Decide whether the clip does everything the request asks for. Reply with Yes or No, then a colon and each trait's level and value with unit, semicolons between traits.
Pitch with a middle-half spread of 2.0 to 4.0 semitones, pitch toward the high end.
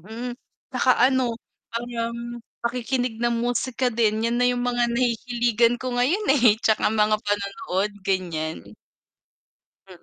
Yes: narrow, 2.4 semitones; high, 235 Hz